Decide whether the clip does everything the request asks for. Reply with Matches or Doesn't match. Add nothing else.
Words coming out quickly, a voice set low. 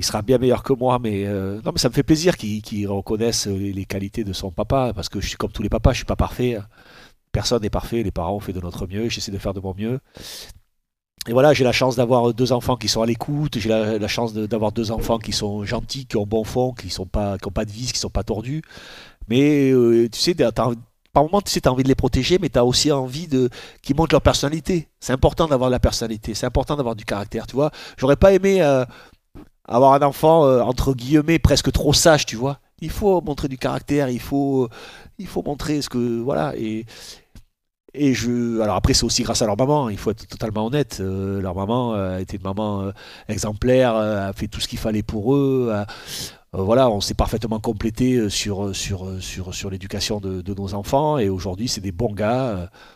Matches